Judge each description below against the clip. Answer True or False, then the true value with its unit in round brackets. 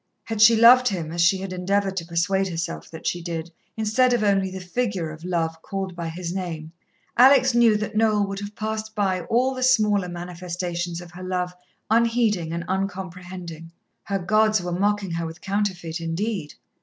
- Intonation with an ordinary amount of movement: True (3.8 semitones)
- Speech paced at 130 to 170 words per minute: False (180 wpm)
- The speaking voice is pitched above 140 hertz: True (190 Hz)